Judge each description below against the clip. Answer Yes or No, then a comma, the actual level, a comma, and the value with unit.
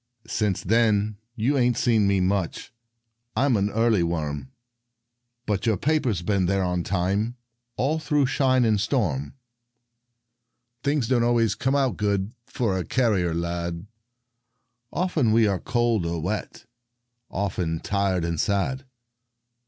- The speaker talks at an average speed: No, slow, 130 wpm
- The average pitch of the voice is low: Yes, low, 105 Hz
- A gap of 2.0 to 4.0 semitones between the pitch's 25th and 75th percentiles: No, average, 4.8 semitones